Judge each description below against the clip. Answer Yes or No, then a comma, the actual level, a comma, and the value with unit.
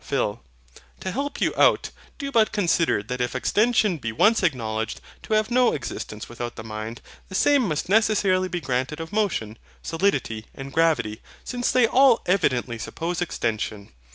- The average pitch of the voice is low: No, medium, 165 Hz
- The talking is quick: No, average, 160 wpm